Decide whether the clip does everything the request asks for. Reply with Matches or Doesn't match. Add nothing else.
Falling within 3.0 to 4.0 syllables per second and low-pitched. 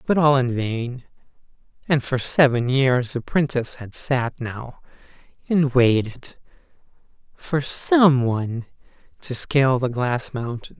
Matches